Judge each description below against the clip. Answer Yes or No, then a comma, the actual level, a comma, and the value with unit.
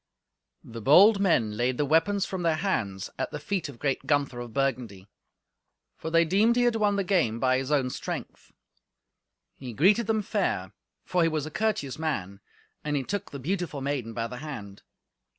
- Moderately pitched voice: Yes, medium, 150 Hz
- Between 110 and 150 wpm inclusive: No, average, 185 wpm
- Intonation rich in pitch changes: Yes, wide, 7.5 semitones